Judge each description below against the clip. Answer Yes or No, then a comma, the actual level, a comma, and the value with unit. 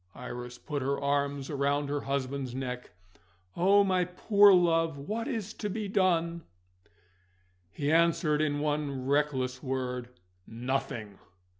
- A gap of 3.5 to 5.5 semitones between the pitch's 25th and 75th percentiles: Yes, average, 4.4 semitones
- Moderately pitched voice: Yes, medium, 145 Hz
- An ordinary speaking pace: No, slow, 125 wpm